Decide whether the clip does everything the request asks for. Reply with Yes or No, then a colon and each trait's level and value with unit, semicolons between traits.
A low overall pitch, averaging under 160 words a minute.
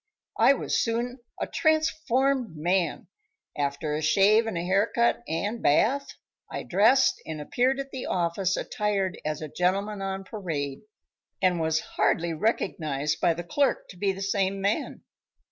No: high, 195 Hz; average, 150 wpm